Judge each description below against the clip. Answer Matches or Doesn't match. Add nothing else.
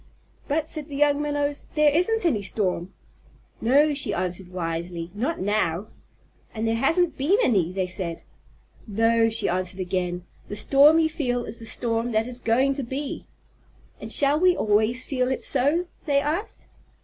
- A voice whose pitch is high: Matches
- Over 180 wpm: Doesn't match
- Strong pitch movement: Matches